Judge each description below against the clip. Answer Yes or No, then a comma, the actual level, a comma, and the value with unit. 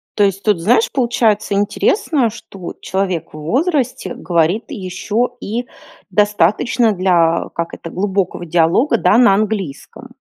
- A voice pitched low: No, high, 205 Hz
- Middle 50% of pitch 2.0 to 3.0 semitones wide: No, average, 4.7 semitones